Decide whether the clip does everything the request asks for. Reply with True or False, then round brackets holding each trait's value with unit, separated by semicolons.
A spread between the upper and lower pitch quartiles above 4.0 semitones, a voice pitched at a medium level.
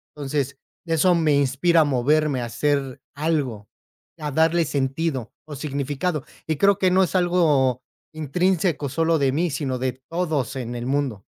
False (3.7 semitones; 145 Hz)